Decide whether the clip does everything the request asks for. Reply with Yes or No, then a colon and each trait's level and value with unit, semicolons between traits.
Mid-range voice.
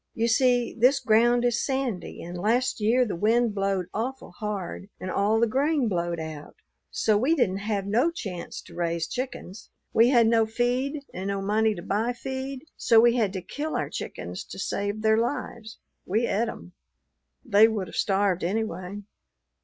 No: high, 220 Hz